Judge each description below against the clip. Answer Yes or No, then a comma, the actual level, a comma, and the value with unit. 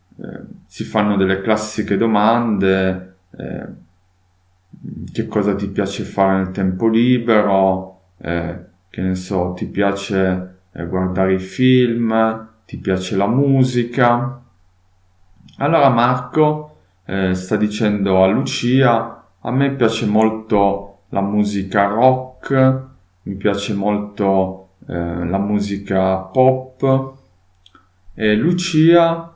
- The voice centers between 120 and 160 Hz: No, low, 100 Hz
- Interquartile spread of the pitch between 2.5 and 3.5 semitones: No, average, 4.0 semitones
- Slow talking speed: Yes, slow, 110 wpm